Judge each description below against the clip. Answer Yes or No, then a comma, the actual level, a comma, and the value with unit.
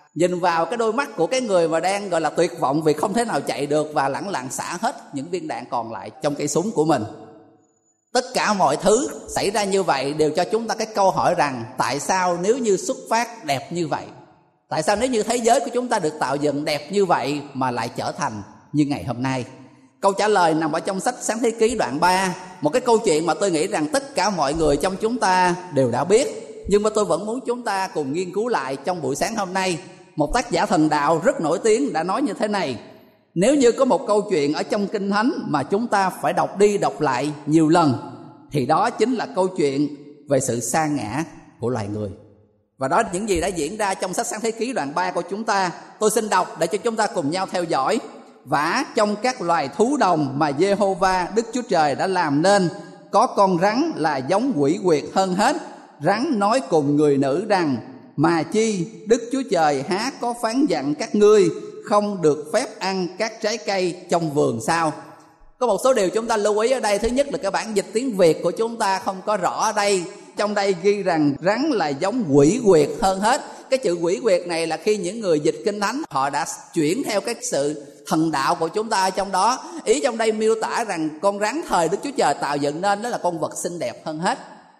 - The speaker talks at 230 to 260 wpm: Yes, average, 240 wpm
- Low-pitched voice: No, high, 190 Hz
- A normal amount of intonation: No, wide, 6.3 semitones